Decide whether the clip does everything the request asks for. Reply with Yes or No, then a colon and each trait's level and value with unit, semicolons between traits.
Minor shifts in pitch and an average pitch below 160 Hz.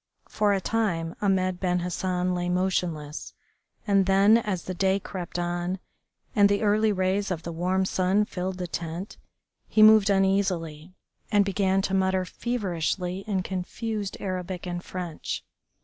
No: narrow, 2.0 semitones; medium, 185 Hz